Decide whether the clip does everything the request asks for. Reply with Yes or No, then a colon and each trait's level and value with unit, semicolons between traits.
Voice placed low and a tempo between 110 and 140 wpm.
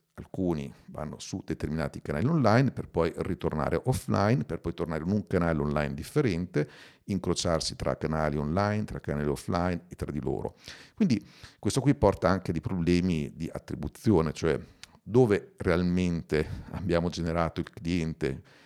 No: very low, 85 Hz; average, 150 wpm